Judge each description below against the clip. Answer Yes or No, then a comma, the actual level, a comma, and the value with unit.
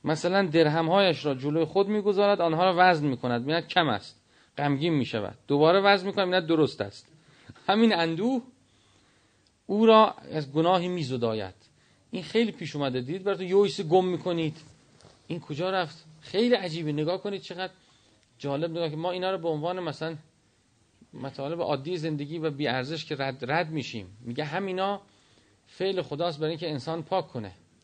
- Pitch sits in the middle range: Yes, medium, 165 Hz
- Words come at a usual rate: No, fast, 170 wpm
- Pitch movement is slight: No, average, 4.7 semitones